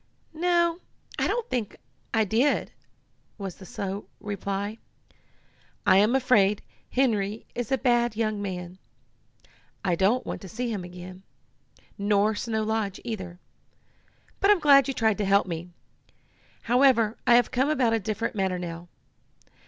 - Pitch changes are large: No, average, 3.9 semitones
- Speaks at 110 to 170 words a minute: Yes, average, 145 wpm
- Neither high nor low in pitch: No, high, 215 Hz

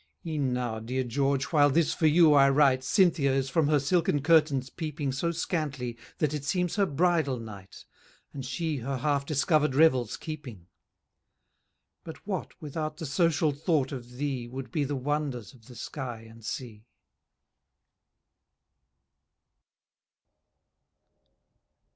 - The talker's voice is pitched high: No, medium, 140 Hz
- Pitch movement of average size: Yes, average, 3.4 semitones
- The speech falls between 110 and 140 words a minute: Yes, slow, 135 wpm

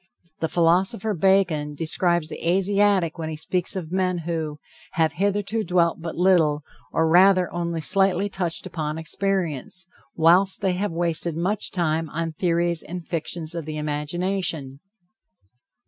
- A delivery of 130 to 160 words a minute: Yes, average, 140 wpm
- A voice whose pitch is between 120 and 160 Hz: No, medium, 170 Hz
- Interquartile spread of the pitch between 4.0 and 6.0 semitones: No, average, 2.8 semitones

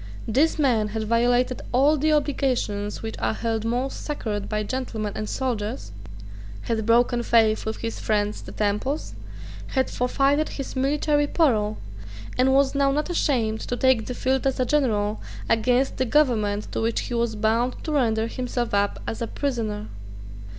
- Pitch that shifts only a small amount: No, average, 3.6 semitones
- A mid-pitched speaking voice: No, high, 240 Hz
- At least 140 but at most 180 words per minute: Yes, average, 165 wpm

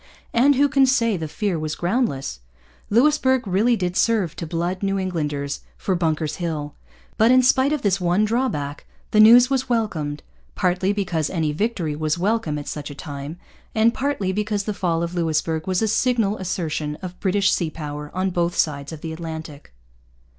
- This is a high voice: No, medium, 180 Hz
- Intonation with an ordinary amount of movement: No, wide, 5.9 semitones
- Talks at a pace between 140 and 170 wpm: No, average, 180 wpm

